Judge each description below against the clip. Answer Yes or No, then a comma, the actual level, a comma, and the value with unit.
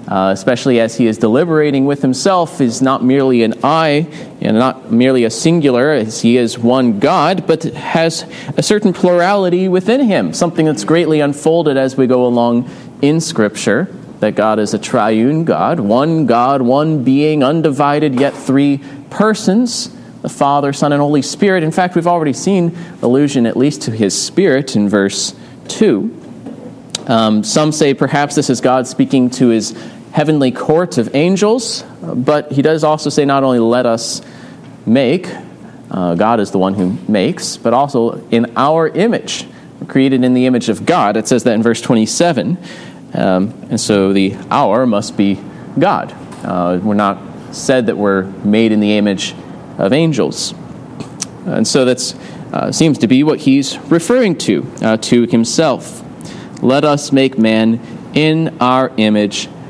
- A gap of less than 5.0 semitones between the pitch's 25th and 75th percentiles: No, average, 5.3 semitones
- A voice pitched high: No, low, 135 Hz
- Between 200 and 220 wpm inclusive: No, average, 165 wpm